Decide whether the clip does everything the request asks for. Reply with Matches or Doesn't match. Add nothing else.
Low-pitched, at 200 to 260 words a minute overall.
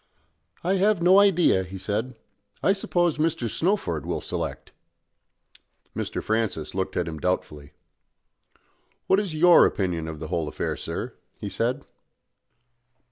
Doesn't match